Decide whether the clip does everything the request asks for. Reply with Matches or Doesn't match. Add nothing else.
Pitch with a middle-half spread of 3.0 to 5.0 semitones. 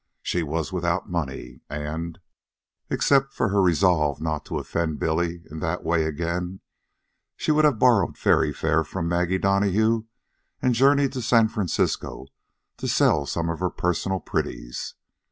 Matches